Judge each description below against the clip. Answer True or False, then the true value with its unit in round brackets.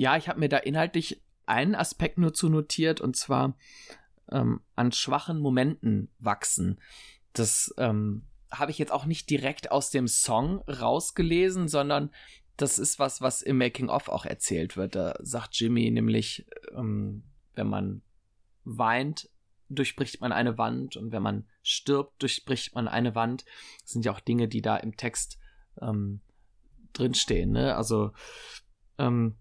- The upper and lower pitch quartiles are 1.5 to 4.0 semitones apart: False (4.4 semitones)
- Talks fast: False (150 wpm)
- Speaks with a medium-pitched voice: False (120 Hz)